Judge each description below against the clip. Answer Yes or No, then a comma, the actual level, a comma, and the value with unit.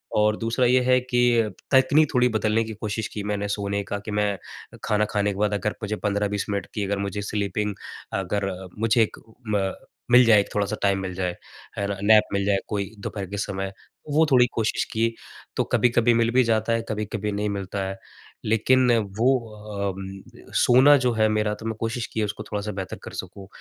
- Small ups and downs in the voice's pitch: Yes, narrow, 2.2 semitones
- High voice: No, low, 105 Hz